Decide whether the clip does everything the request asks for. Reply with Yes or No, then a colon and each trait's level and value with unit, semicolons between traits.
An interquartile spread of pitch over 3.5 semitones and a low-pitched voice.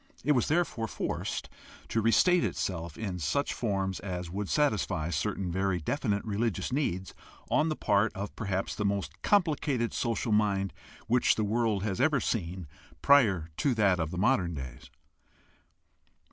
Yes: average, 4.6 semitones; low, 105 Hz